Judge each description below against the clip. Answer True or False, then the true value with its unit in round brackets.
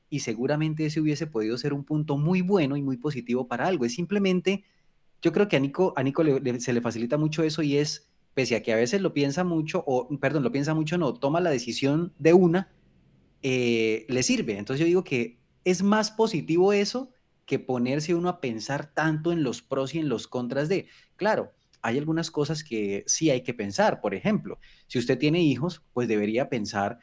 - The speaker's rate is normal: False (210 wpm)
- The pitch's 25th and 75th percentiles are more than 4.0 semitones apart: True (5.1 semitones)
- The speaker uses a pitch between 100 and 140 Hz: False (150 Hz)